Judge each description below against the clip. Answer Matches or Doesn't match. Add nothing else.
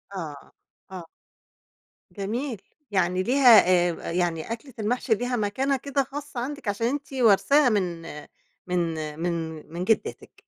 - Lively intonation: Matches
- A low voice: Doesn't match